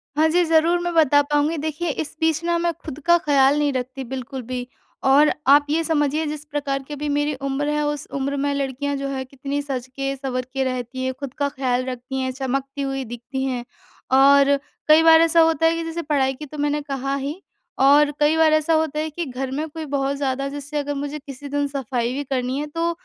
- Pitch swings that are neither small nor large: No, narrow, 2.2 semitones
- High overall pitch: Yes, very high, 285 Hz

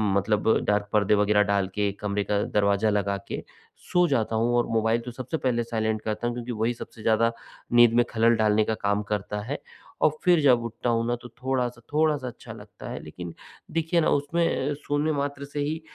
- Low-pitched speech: Yes, low, 115 Hz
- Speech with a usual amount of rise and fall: Yes, average, 4.0 semitones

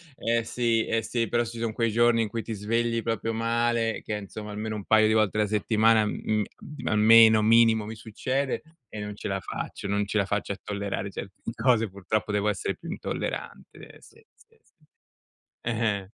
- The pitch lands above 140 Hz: No, low, 110 Hz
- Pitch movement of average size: No, narrow, 1.7 semitones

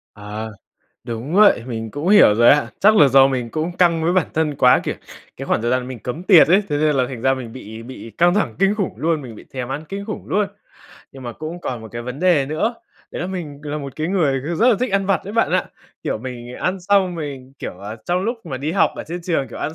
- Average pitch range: No, wide, 6.3 semitones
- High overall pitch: No, medium, 150 Hz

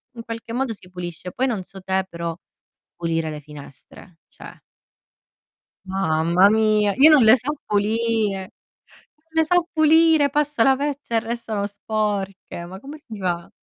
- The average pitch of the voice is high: Yes, high, 215 Hz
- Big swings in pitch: Yes, wide, 6.0 semitones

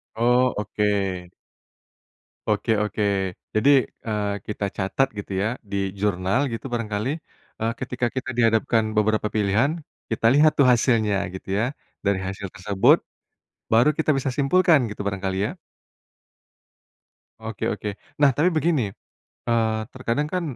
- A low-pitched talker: Yes, low, 110 Hz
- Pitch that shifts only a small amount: No, average, 4.1 semitones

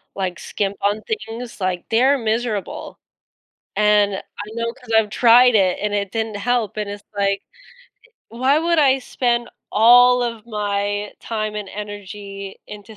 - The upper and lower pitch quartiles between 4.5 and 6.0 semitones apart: No, average, 2.8 semitones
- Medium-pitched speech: No, high, 215 Hz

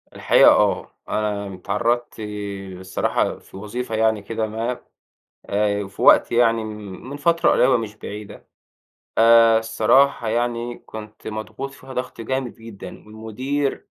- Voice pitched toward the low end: Yes, low, 110 Hz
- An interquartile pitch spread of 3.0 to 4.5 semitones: No, narrow, 2.5 semitones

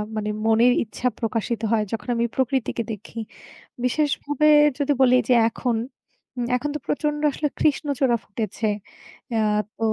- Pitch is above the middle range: Yes, high, 245 Hz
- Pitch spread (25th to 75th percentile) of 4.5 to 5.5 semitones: No, average, 4.0 semitones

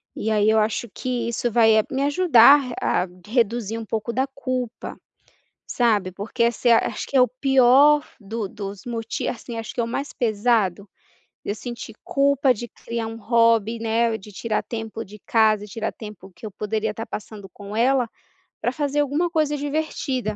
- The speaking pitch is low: No, high, 230 Hz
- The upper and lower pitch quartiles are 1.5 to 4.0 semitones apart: Yes, average, 3.0 semitones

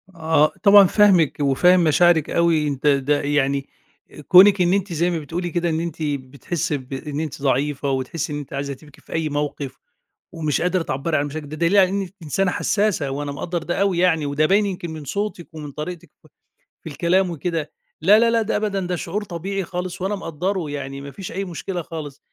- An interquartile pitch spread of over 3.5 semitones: Yes, average, 4.0 semitones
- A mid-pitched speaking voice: Yes, medium, 165 Hz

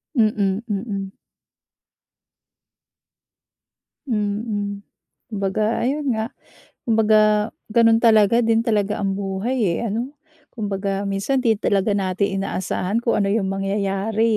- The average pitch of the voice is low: No, high, 210 Hz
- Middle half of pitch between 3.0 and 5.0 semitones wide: No, narrow, 2.4 semitones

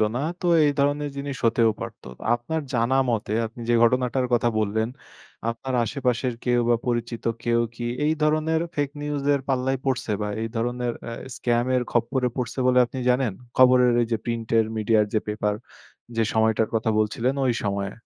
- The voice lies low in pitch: Yes, low, 120 Hz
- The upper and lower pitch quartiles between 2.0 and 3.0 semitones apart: Yes, narrow, 2.6 semitones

